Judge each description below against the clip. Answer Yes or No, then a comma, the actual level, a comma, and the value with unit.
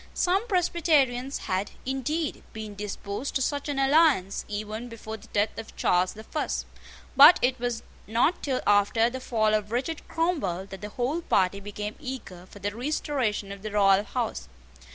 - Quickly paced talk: No, average, 170 wpm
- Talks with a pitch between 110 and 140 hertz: No, high, 230 Hz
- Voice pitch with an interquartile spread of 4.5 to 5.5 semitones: Yes, average, 5.2 semitones